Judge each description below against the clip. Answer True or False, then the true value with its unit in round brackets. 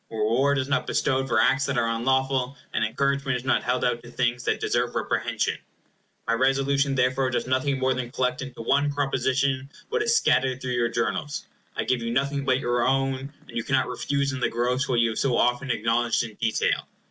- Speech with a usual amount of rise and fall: False (2.2 semitones)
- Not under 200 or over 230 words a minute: True (205 wpm)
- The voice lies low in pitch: True (130 Hz)